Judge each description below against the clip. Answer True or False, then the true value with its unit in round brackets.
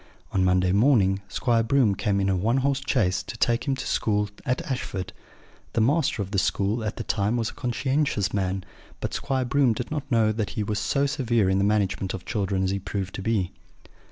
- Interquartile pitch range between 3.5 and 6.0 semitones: True (4.4 semitones)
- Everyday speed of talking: False (215 wpm)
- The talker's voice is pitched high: False (110 Hz)